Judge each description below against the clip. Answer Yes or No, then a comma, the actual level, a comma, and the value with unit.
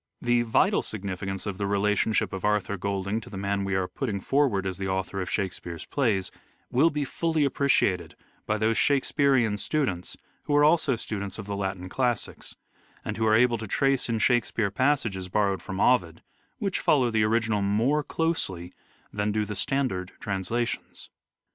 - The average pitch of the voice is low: Yes, low, 105 Hz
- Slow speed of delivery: No, average, 175 wpm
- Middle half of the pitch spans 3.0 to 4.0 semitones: No, average, 4.4 semitones